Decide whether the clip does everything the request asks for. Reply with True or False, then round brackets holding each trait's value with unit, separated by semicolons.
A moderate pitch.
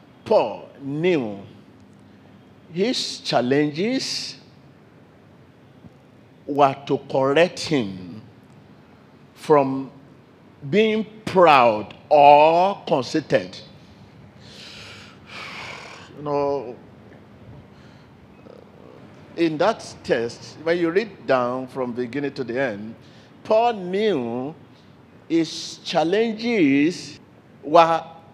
True (145 Hz)